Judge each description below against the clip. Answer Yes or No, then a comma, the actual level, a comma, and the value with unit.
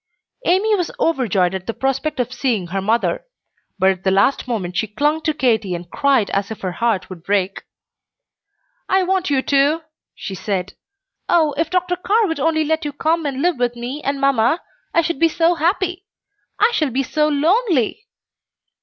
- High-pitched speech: Yes, very high, 275 Hz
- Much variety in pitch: Yes, wide, 7.2 semitones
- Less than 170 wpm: No, average, 190 wpm